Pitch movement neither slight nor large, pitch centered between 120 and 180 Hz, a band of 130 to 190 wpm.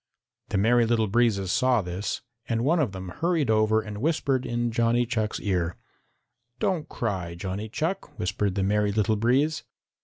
No: average, 3.5 semitones; low, 110 Hz; average, 160 wpm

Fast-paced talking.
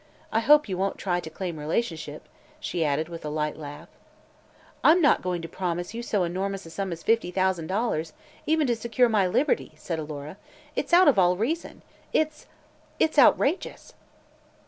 No: average, 175 wpm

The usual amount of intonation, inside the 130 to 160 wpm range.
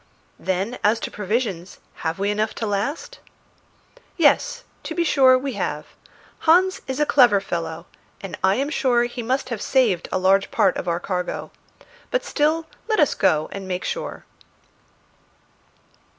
No: wide, 7.0 semitones; average, 155 wpm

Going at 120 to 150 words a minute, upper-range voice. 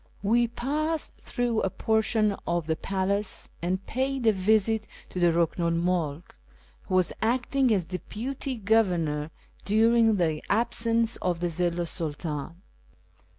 Yes: average, 140 wpm; high, 200 Hz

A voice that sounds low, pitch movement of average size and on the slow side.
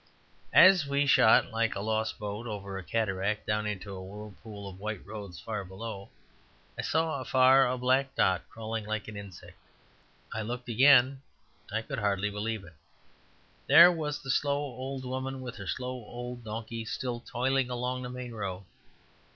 No: low, 115 Hz; average, 3.8 semitones; average, 165 wpm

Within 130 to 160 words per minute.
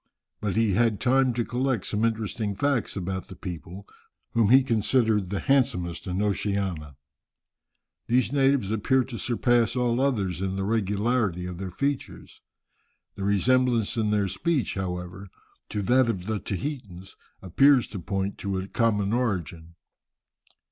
Yes: average, 145 wpm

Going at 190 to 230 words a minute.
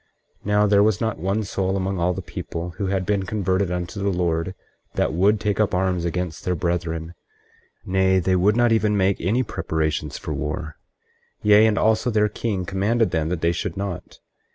Yes: average, 195 wpm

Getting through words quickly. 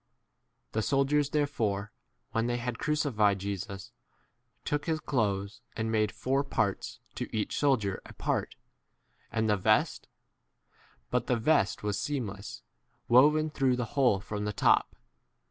No: average, 145 wpm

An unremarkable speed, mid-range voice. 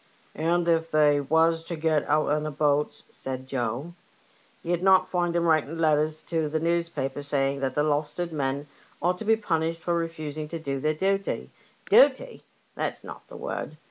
Yes: average, 180 wpm; medium, 155 Hz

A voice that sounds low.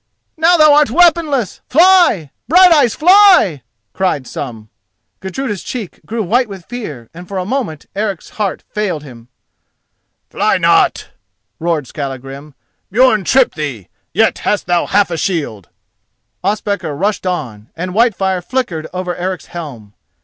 No: high, 190 Hz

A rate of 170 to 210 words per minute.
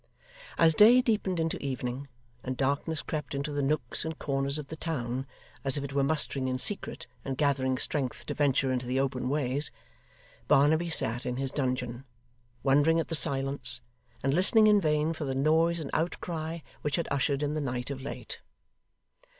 Yes: average, 180 wpm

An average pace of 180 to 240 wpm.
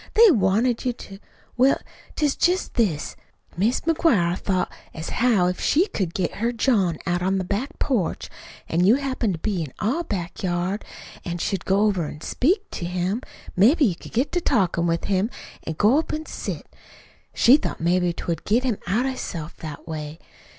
Yes: average, 190 wpm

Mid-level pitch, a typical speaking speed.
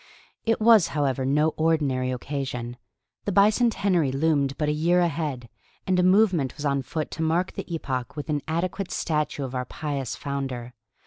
Yes: medium, 150 Hz; average, 170 wpm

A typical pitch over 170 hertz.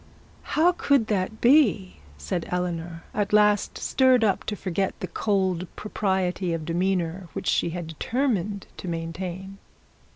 Yes: high, 190 Hz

